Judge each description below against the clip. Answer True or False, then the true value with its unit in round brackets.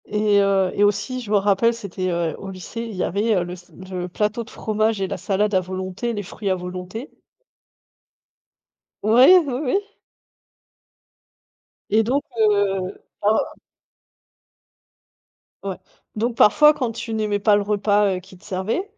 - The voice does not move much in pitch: False (3.2 semitones)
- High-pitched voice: True (205 Hz)